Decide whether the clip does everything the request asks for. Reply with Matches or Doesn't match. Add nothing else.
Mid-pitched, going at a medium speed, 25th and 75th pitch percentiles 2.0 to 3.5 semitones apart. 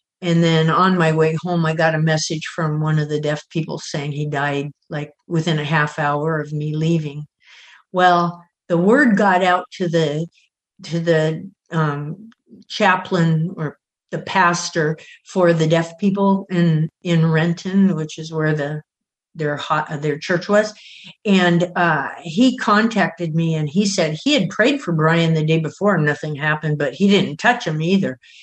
Matches